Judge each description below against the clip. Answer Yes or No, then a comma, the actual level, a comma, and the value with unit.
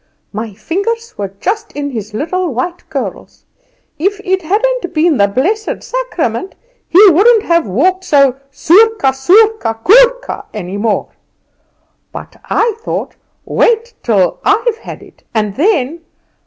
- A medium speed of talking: No, slow, 130 wpm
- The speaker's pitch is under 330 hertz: No, very high, 345 Hz